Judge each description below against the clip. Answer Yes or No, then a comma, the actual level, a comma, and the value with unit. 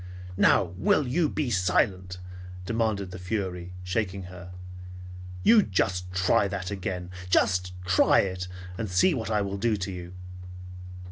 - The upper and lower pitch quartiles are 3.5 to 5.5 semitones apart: No, average, 2.7 semitones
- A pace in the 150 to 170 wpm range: No, average, 140 wpm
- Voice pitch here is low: Yes, very low, 95 Hz